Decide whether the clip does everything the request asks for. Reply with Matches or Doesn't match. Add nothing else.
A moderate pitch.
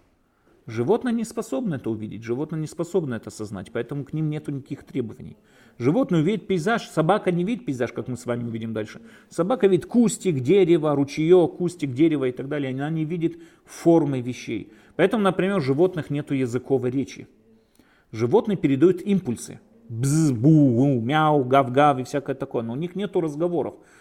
Matches